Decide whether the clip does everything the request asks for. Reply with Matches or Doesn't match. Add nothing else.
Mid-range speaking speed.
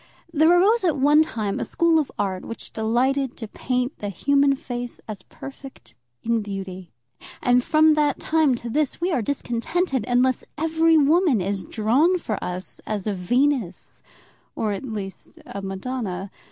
Matches